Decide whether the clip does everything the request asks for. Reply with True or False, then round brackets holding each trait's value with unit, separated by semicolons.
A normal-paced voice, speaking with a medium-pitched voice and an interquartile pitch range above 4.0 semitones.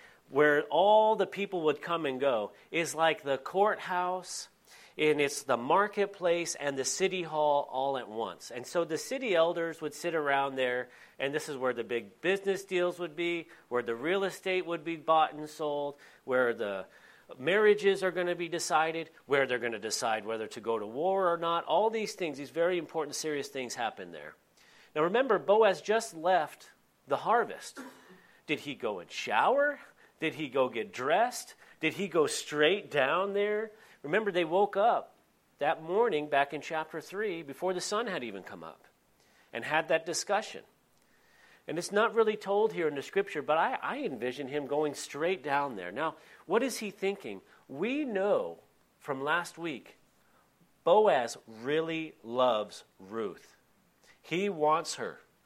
True (175 wpm; 165 Hz; 5.4 semitones)